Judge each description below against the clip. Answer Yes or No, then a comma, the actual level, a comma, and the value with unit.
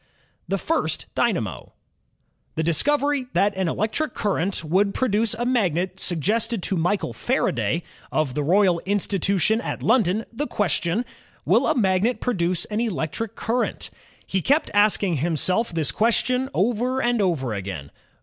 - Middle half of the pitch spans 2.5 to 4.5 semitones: No, average, 5.2 semitones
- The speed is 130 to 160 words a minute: Yes, average, 140 wpm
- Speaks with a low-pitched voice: No, high, 200 Hz